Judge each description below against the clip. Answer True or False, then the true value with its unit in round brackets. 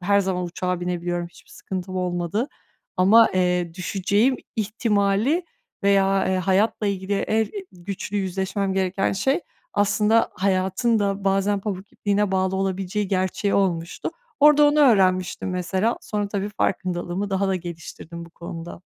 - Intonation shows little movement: True (2.1 semitones)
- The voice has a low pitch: False (195 Hz)